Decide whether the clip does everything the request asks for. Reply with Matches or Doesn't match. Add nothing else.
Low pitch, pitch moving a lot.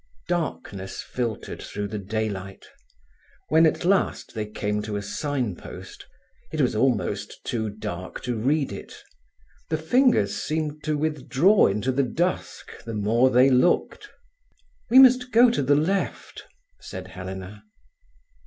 Matches